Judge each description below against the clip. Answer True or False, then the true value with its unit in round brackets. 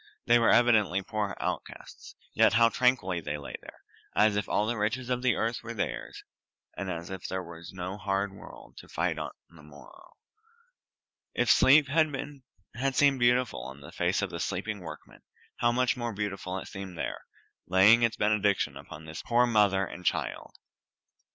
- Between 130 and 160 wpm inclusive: False (175 wpm)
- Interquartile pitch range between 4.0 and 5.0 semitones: True (4.4 semitones)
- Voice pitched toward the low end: True (105 Hz)